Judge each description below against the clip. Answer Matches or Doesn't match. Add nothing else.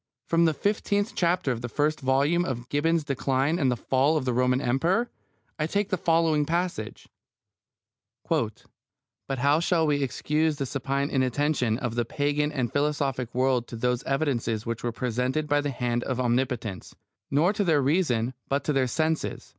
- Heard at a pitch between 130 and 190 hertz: Matches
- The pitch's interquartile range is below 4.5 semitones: Matches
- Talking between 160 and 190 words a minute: Matches